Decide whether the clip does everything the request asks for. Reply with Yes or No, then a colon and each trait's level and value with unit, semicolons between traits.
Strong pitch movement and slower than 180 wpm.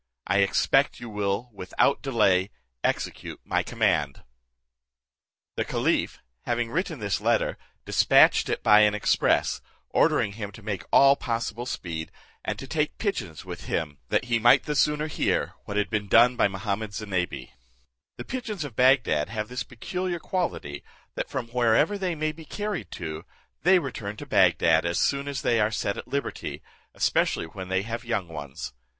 Yes: wide, 6.3 semitones; average, 170 wpm